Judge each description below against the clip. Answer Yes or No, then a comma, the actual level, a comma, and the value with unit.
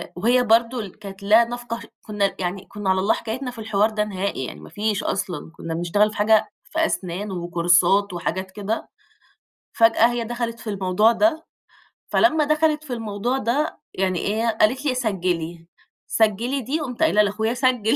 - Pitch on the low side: No, high, 215 Hz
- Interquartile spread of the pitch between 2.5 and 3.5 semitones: No, average, 3.9 semitones